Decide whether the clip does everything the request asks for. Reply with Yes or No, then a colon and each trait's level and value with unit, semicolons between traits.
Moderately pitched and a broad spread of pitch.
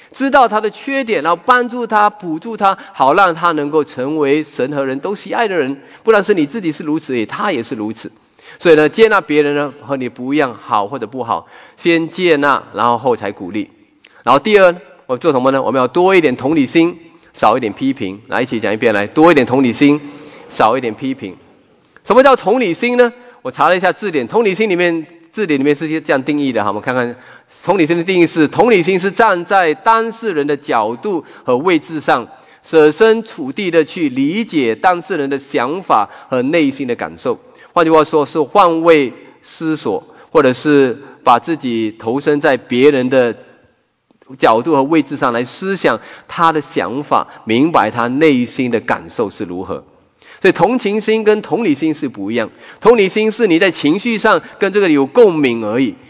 Yes: medium, 165 Hz; wide, 7.3 semitones